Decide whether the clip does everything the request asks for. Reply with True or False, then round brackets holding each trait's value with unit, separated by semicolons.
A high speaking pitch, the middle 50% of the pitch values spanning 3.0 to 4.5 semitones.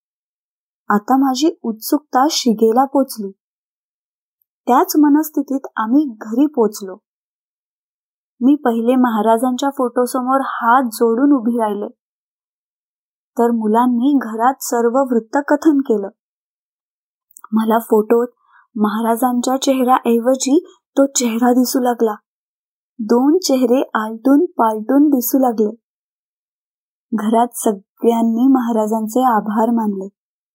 True (245 Hz; 3.3 semitones)